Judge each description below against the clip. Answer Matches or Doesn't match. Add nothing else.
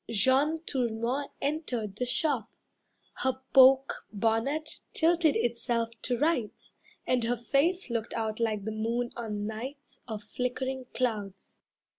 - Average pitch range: Matches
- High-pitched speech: Matches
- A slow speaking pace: Matches